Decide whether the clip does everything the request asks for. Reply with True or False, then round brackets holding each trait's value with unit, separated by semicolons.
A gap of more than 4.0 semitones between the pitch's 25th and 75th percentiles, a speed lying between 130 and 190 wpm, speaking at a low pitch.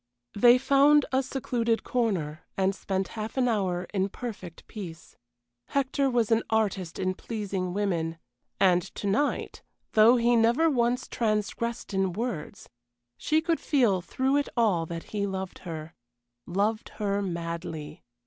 False (4.6 semitones; 140 wpm; 210 Hz)